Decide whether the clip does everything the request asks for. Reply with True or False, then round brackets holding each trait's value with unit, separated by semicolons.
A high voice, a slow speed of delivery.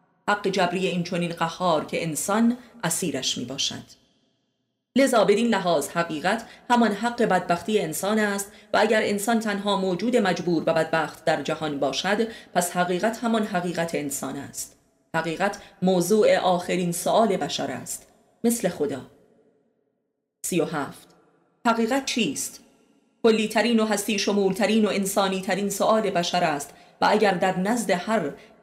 False (200 Hz; 140 wpm)